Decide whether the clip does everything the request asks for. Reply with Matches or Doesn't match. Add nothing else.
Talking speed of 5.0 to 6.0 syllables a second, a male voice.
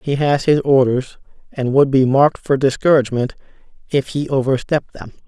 Matches